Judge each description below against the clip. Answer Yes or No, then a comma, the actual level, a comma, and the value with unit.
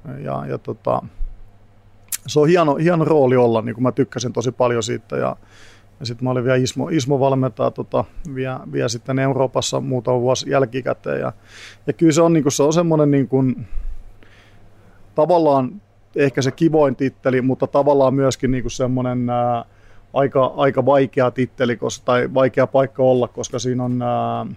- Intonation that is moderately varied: Yes, average, 3.2 semitones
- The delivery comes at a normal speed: No, fast, 165 wpm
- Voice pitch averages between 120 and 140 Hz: Yes, low, 125 Hz